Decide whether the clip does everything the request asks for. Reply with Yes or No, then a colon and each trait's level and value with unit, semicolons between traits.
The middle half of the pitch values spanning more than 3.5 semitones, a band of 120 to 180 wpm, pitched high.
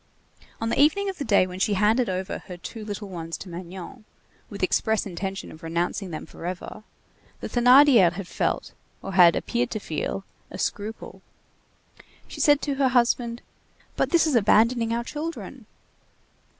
Yes: average, 5.1 semitones; average, 165 wpm; high, 210 Hz